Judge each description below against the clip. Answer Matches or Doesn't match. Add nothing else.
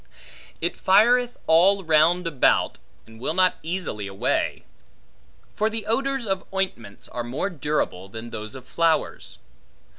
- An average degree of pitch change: Doesn't match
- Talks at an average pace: Doesn't match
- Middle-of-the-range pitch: Matches